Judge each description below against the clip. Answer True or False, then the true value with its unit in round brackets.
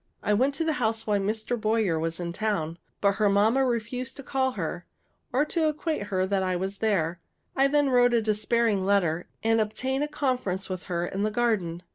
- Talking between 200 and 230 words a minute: True (205 wpm)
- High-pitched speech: True (215 Hz)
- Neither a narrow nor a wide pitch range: True (4.9 semitones)